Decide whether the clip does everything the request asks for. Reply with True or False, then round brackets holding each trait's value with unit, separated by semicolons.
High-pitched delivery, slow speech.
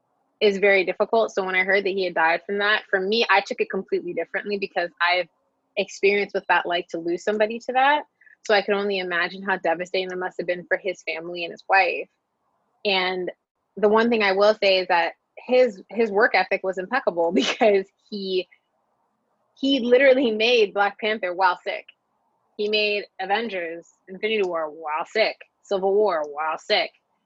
False (195 Hz; 185 wpm)